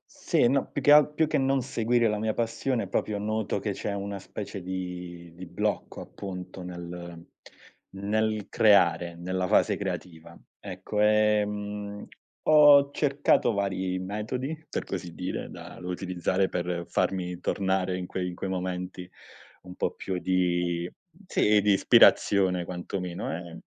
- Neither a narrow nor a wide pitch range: Yes, average, 3.0 semitones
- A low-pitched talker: Yes, very low, 95 Hz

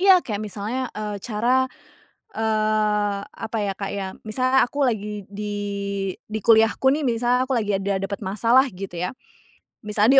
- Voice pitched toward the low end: No, high, 215 Hz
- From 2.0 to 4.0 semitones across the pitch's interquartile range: Yes, average, 3.1 semitones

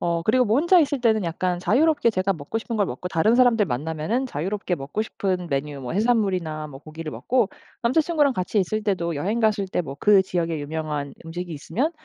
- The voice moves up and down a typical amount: No, wide, 6.1 semitones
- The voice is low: No, high, 190 Hz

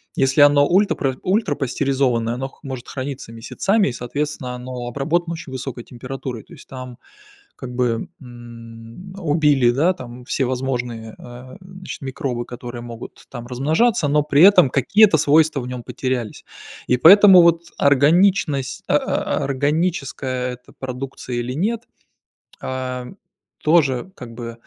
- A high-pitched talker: No, low, 130 Hz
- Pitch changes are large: No, average, 3.8 semitones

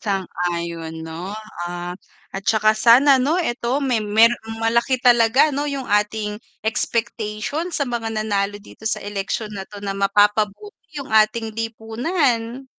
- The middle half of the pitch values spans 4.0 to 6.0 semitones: No, average, 3.0 semitones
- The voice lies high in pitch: Yes, high, 220 Hz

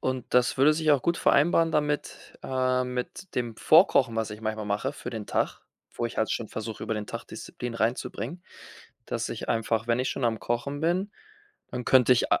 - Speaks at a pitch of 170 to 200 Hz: No, low, 125 Hz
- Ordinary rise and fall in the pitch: Yes, average, 4.4 semitones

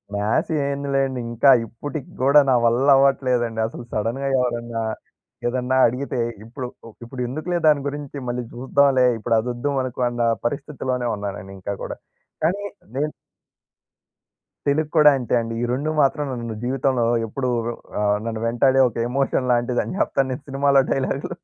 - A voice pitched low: Yes, low, 130 Hz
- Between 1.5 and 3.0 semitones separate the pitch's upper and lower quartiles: Yes, average, 2.7 semitones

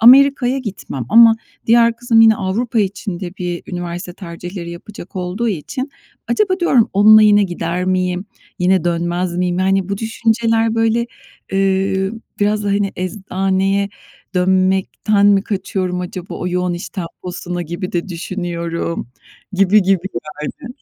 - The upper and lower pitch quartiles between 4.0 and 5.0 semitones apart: No, average, 3.3 semitones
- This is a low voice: No, high, 190 Hz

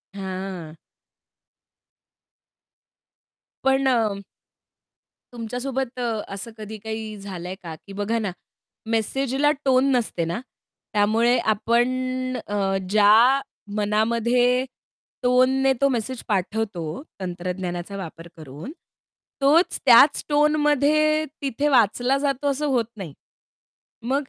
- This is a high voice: Yes, high, 230 Hz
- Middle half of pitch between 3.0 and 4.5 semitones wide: No, average, 5.1 semitones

